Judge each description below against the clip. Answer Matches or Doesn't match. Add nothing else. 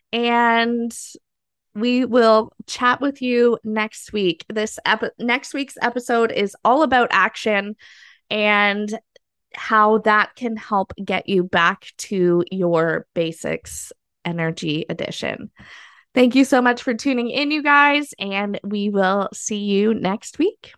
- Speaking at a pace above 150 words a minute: Doesn't match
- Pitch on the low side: Doesn't match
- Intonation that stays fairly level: Doesn't match